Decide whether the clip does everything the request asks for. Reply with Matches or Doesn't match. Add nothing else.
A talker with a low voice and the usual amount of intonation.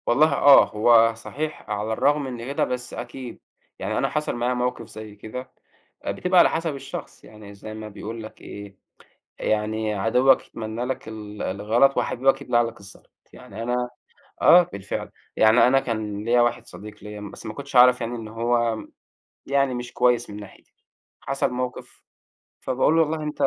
Matches